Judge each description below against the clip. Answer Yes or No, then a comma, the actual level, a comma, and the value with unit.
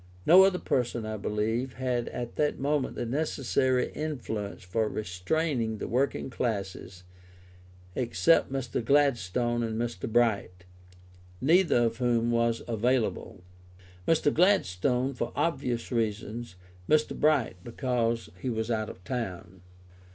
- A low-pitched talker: Yes, low, 120 Hz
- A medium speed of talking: No, slow, 120 wpm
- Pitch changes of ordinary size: Yes, average, 3.4 semitones